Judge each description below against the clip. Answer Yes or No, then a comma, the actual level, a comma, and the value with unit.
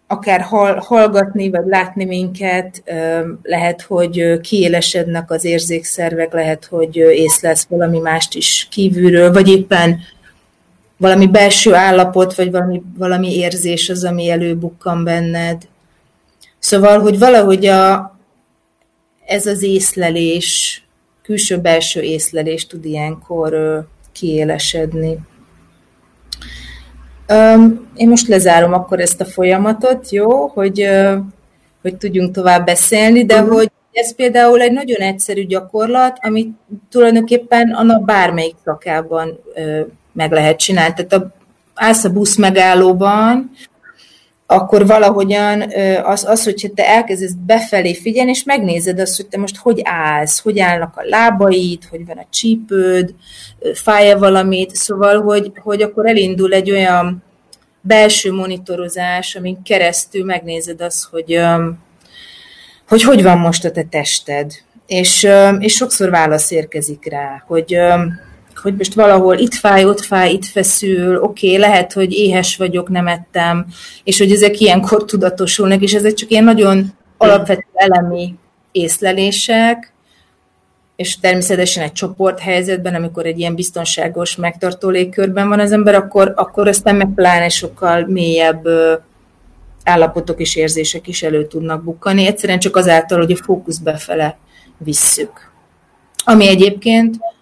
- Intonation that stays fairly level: No, average, 3.2 semitones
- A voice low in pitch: No, medium, 185 Hz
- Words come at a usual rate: Yes, average, 125 wpm